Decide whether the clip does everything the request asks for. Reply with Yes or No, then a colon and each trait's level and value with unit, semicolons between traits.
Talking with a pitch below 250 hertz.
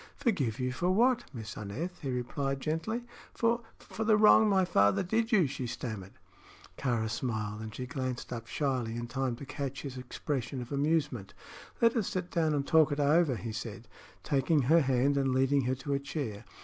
Yes: low, 135 Hz